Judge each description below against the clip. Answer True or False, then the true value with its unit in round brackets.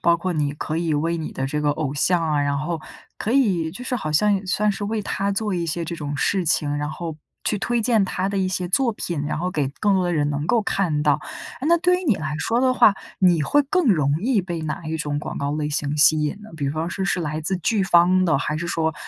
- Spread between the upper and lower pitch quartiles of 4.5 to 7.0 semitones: True (4.8 semitones)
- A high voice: False (170 Hz)